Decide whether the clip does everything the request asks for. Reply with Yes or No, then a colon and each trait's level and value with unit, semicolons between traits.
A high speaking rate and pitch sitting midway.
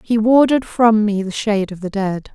No: fast, 230 wpm; high, 215 Hz